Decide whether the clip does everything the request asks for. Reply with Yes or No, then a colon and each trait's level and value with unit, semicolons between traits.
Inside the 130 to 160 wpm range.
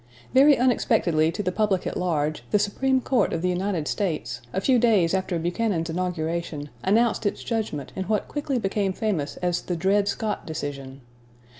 No: average, 170 wpm